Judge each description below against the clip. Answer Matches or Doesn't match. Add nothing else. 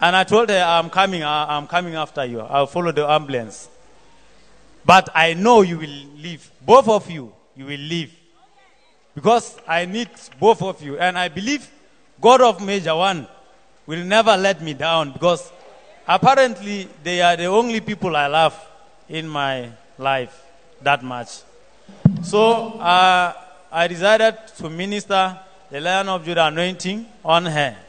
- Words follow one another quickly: Doesn't match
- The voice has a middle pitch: Matches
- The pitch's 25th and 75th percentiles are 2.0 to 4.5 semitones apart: Matches